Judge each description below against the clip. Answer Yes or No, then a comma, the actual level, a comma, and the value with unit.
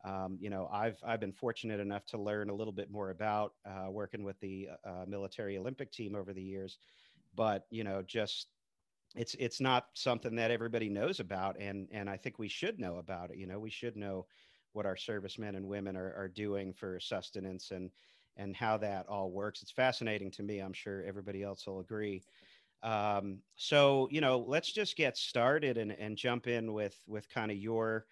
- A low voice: Yes, low, 100 Hz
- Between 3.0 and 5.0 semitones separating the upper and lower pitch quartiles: No, narrow, 2.6 semitones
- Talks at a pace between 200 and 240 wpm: Yes, fast, 205 wpm